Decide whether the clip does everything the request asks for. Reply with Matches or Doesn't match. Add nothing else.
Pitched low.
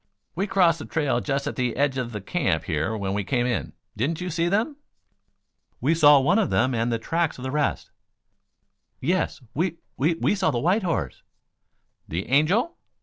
Doesn't match